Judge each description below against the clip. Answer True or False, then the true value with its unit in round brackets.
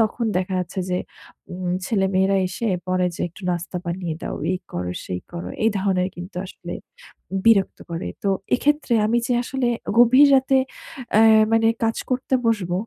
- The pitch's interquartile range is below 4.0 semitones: False (4.3 semitones)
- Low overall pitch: False (195 Hz)